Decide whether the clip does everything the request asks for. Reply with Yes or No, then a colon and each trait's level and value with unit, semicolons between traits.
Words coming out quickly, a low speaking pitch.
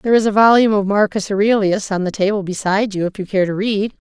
No: fast, 250 wpm; high, 205 Hz